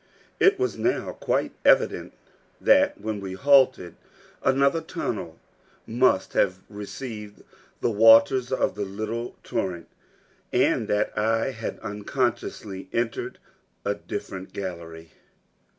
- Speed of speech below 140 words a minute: Yes, slow, 110 wpm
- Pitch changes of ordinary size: Yes, average, 4.9 semitones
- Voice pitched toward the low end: Yes, low, 110 Hz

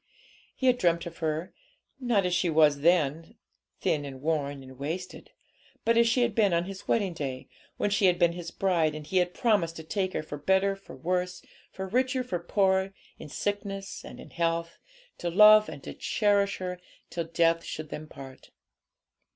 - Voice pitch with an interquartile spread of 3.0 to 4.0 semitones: Yes, average, 3.7 semitones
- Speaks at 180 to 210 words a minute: Yes, average, 190 wpm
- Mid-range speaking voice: Yes, medium, 175 Hz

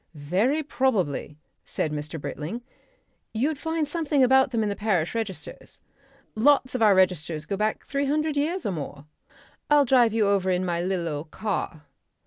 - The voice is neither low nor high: No, high, 215 Hz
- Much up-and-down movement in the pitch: Yes, wide, 7.7 semitones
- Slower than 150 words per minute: No, average, 165 wpm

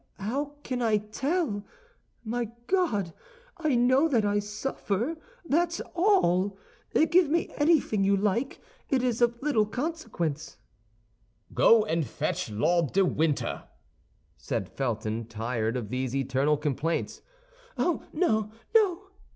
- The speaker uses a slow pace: Yes, slow, 125 wpm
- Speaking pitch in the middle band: No, high, 215 Hz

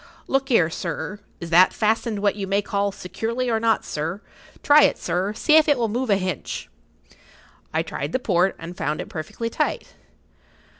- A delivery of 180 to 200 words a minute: Yes, average, 185 wpm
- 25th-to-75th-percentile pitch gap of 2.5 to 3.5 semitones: No, average, 4.5 semitones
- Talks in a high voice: Yes, high, 205 Hz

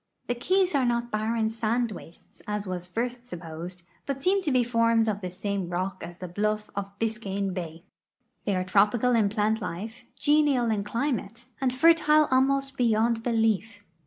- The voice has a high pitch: Yes, high, 225 Hz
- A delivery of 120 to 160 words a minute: No, average, 175 wpm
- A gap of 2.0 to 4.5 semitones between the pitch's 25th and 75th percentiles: Yes, average, 3.8 semitones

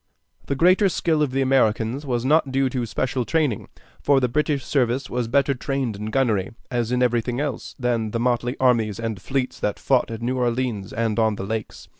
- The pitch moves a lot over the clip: No, average, 2.9 semitones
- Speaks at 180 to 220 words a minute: Yes, average, 200 wpm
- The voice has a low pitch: Yes, low, 125 Hz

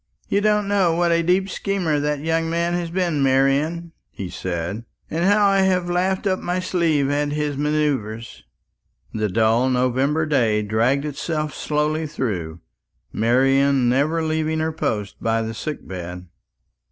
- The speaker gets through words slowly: No, average, 155 wpm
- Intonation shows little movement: No, wide, 5.6 semitones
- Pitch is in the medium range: Yes, medium, 150 Hz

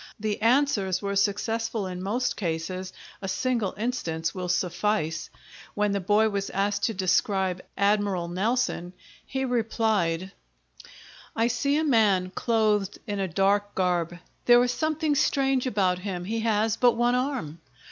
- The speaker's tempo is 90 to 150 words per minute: Yes, average, 145 wpm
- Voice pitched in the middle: No, high, 205 Hz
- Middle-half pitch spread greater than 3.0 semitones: Yes, average, 3.9 semitones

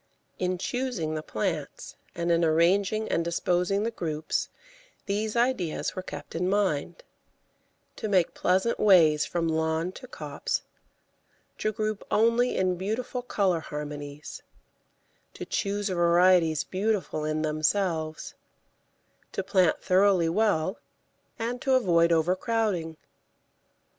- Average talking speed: No, slow, 115 wpm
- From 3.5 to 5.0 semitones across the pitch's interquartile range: Yes, average, 4.5 semitones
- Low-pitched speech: No, medium, 185 Hz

